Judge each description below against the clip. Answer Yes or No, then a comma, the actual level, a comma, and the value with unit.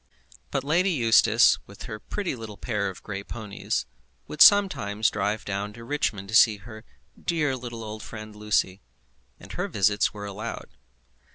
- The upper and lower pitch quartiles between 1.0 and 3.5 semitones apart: Yes, average, 2.9 semitones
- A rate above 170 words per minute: No, average, 160 wpm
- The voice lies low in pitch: Yes, low, 110 Hz